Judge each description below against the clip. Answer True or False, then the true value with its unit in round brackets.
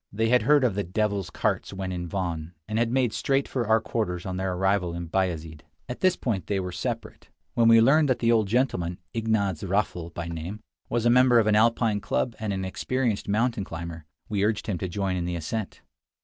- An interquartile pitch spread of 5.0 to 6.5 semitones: False (4.4 semitones)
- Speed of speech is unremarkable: False (220 wpm)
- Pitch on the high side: False (100 Hz)